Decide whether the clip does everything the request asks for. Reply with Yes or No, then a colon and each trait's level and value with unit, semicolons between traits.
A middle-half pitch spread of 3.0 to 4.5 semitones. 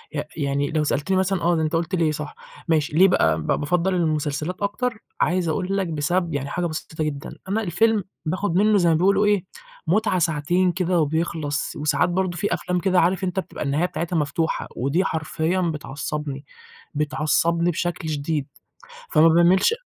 Yes: average, 3.4 semitones